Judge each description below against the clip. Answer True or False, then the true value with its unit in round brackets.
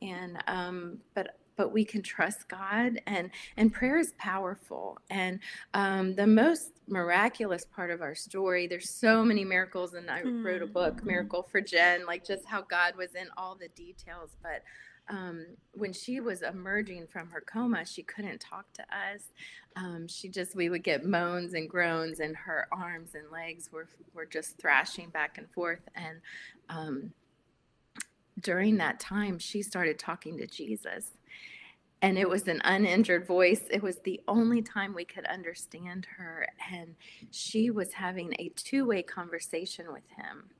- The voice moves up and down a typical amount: True (3.1 semitones)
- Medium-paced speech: True (165 wpm)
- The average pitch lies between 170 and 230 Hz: True (185 Hz)